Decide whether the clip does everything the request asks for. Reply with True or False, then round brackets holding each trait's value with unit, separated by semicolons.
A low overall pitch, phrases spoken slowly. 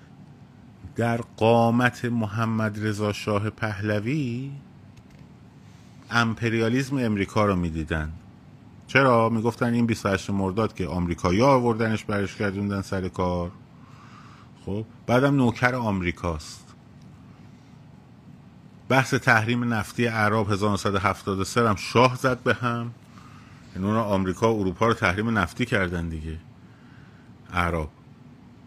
True (110 Hz; 100 wpm)